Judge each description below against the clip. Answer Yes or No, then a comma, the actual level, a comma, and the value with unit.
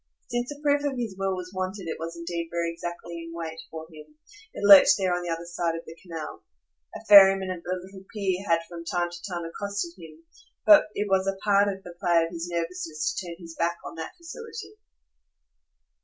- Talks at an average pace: No, fast, 215 wpm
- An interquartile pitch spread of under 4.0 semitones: Yes, average, 2.7 semitones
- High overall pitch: No, medium, 175 Hz